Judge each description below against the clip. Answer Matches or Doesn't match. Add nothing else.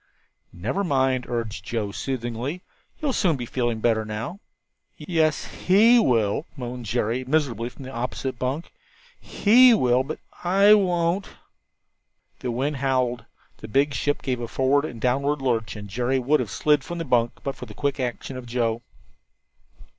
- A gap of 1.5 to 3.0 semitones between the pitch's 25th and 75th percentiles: Doesn't match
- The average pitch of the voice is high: Doesn't match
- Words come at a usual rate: Matches